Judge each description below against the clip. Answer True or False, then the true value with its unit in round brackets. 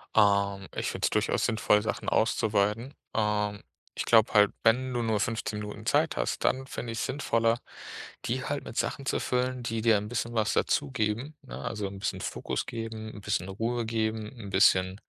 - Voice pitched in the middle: False (110 Hz)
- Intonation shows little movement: True (2.3 semitones)